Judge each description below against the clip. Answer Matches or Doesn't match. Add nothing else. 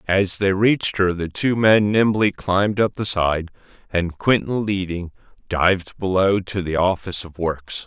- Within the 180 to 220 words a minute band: Doesn't match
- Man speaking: Matches